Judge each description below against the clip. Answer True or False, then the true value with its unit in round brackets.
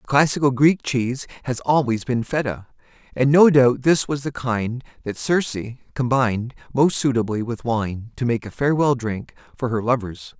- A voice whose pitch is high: False (125 Hz)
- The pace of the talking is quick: False (175 wpm)